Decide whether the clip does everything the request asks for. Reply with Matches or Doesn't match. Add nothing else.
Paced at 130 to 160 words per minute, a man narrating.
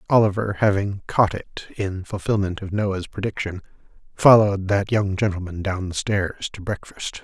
Matches